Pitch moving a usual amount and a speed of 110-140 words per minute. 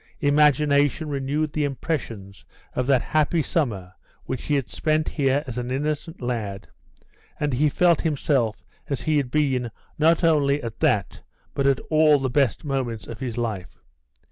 No: average, 3.7 semitones; average, 160 wpm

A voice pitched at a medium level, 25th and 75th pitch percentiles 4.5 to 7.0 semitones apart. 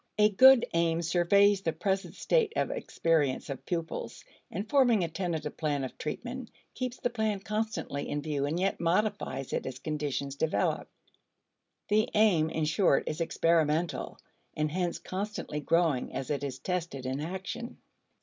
Yes: medium, 170 Hz; wide, 5.5 semitones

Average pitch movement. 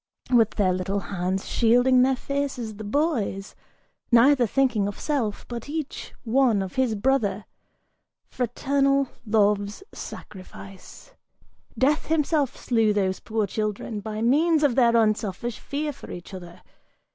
Yes: average, 4.9 semitones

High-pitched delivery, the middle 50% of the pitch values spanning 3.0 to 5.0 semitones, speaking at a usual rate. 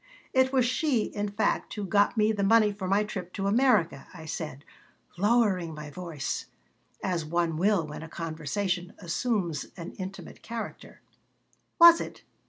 Yes: high, 195 Hz; average, 4.4 semitones; average, 155 wpm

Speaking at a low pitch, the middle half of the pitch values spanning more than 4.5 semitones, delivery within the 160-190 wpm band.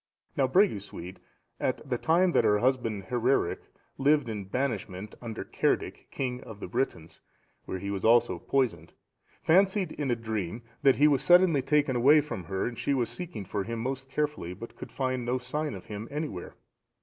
Yes: low, 125 Hz; wide, 5.5 semitones; average, 180 wpm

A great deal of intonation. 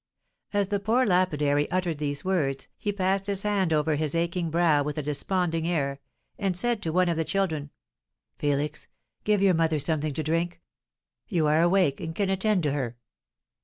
No: average, 4.2 semitones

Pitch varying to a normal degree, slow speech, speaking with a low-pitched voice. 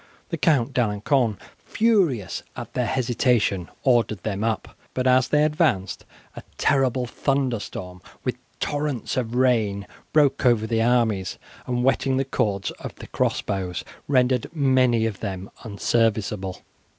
Yes: average, 4.0 semitones; slow, 130 wpm; low, 120 Hz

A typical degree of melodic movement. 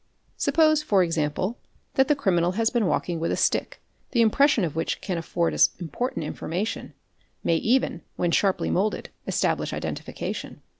No: wide, 6.1 semitones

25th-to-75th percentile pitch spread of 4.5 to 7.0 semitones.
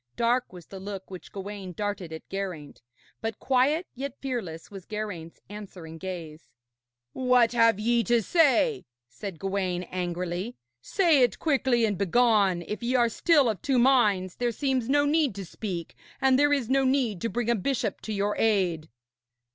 Yes: average, 5.3 semitones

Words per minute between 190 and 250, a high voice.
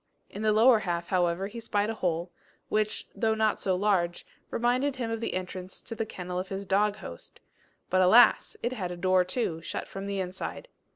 Yes: fast, 205 wpm; high, 195 Hz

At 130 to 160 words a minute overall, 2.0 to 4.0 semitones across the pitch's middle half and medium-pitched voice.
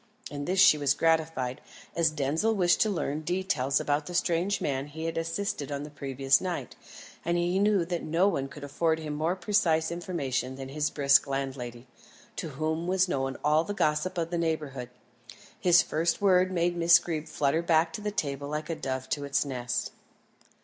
No: average, 190 wpm; average, 3.7 semitones; medium, 160 Hz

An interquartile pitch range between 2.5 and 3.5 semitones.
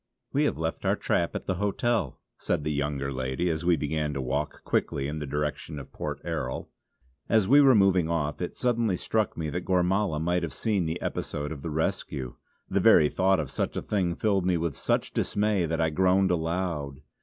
No: average, 4.2 semitones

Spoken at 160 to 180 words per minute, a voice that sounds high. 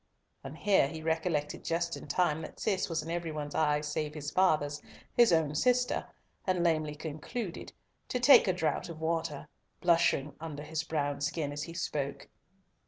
No: average, 170 wpm; medium, 160 Hz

